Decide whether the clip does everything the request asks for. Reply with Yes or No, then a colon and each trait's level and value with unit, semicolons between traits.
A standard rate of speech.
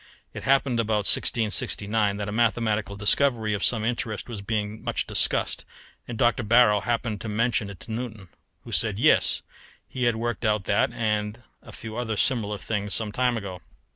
Yes: average, 175 wpm